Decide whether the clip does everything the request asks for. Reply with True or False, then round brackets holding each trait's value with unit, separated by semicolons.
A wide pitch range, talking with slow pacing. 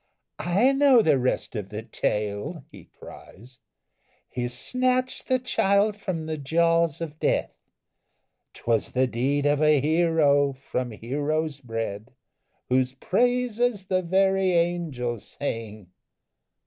True (6.9 semitones; 120 wpm)